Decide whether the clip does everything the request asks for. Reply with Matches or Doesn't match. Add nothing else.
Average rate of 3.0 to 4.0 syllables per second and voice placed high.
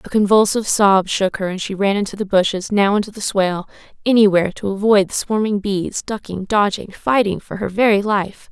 Doesn't match